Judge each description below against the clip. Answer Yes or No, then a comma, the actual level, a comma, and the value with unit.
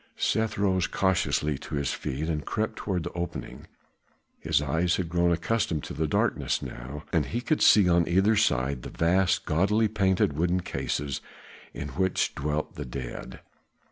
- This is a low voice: Yes, very low, 85 Hz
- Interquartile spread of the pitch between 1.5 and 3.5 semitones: No, average, 4.4 semitones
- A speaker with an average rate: Yes, average, 165 wpm